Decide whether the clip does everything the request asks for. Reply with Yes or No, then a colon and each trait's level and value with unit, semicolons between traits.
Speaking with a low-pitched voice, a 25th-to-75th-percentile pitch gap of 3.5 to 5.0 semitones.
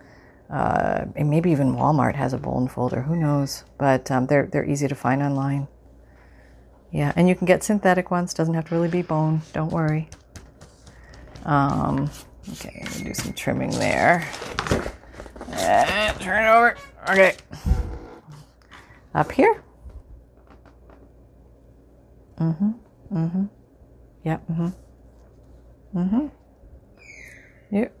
No: medium, 155 Hz; average, 4.7 semitones